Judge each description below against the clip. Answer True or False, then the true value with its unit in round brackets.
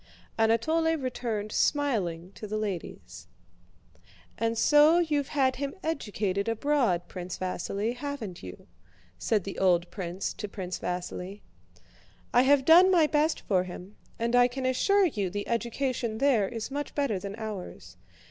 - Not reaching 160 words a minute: True (145 wpm)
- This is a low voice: False (230 Hz)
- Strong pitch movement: True (6.4 semitones)